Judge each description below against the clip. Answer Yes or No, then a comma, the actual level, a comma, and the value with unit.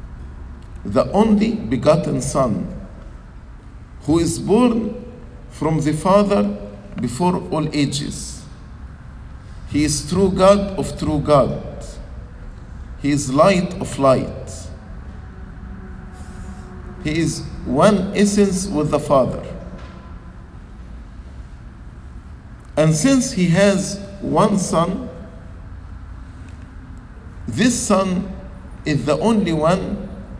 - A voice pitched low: No, medium, 145 Hz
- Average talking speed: No, slow, 85 wpm